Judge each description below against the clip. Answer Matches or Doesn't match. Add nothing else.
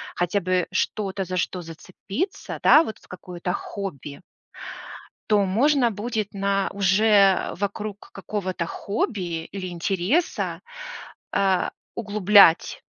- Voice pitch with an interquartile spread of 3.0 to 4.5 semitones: Doesn't match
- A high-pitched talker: Matches